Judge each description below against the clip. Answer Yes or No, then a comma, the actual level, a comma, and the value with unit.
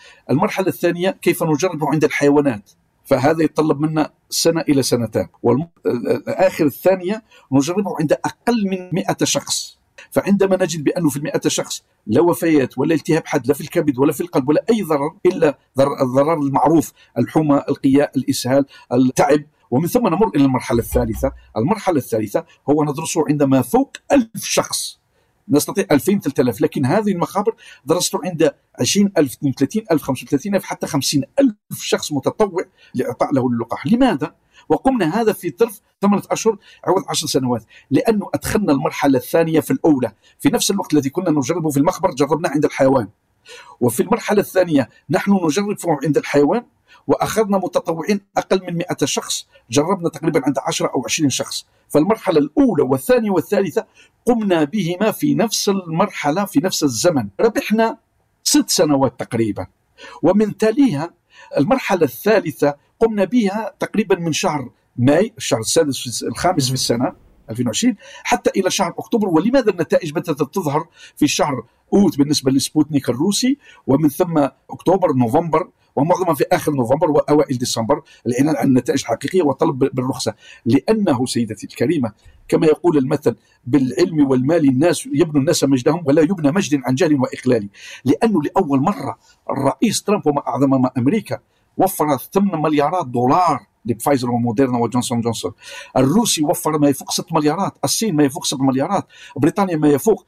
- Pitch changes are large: Yes, wide, 5.7 semitones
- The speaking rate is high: Yes, fast, 140 wpm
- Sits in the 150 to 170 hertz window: Yes, medium, 160 Hz